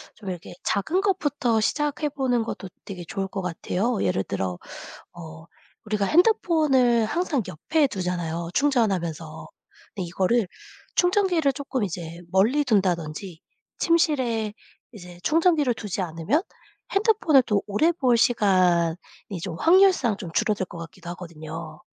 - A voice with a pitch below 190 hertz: No, high, 210 Hz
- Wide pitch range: Yes, wide, 8.7 semitones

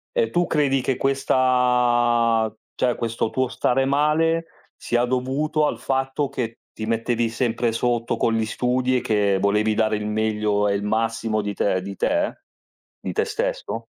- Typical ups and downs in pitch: Yes, average, 3.4 semitones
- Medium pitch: No, low, 120 Hz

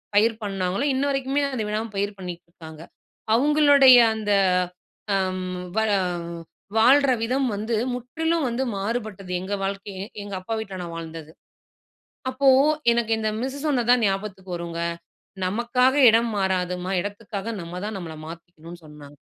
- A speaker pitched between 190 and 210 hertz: Yes, high, 205 Hz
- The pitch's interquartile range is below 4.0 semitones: No, average, 4.9 semitones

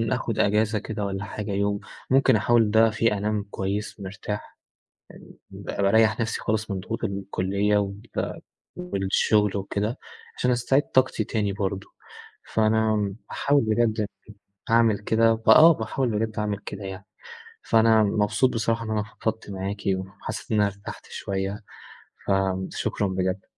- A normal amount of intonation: No, narrow, 2.1 semitones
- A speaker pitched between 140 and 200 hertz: No, low, 105 Hz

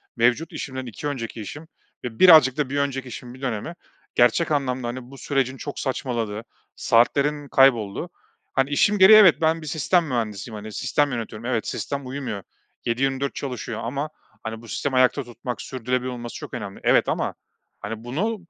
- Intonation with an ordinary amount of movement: Yes, average, 3.5 semitones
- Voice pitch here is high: No, low, 130 Hz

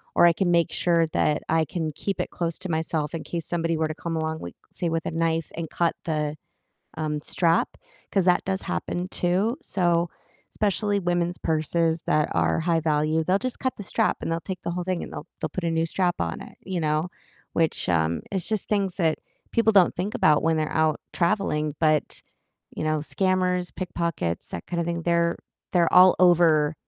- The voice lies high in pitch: No, medium, 170 Hz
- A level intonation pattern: Yes, narrow, 2.3 semitones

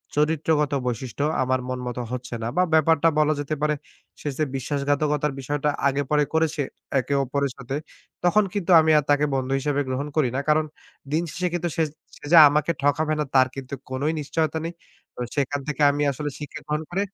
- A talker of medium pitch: Yes, medium, 150 Hz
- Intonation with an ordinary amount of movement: No, narrow, 2.3 semitones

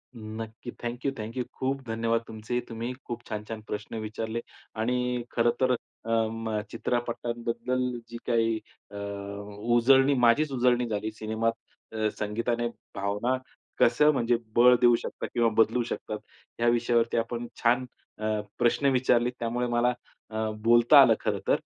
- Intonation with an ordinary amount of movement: No, narrow, 1.5 semitones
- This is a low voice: Yes, low, 115 Hz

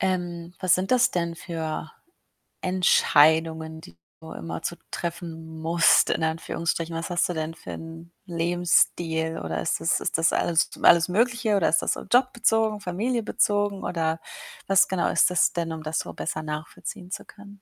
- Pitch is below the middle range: No, medium, 170 Hz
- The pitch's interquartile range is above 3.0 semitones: No, average, 2.7 semitones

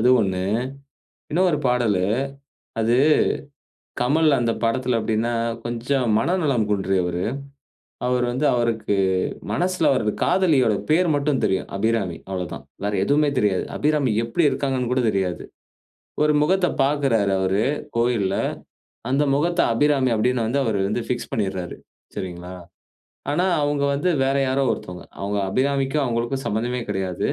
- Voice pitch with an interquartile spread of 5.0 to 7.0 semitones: Yes, wide, 5.5 semitones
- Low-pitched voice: Yes, low, 120 Hz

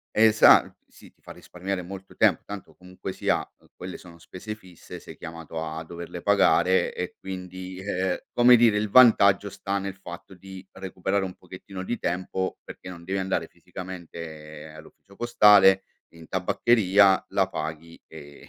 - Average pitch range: No, narrow, 2.1 semitones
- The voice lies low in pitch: Yes, very low, 95 Hz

